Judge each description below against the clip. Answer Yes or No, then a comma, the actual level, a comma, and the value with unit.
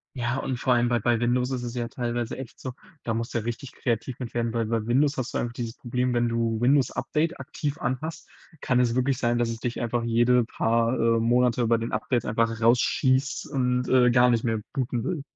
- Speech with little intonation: Yes, narrow, 1.6 semitones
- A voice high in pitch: No, low, 120 Hz